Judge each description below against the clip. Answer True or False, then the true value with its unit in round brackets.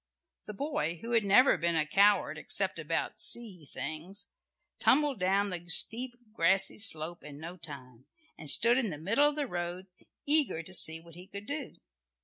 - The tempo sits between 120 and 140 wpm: False (175 wpm)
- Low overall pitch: False (190 Hz)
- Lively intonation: True (6.0 semitones)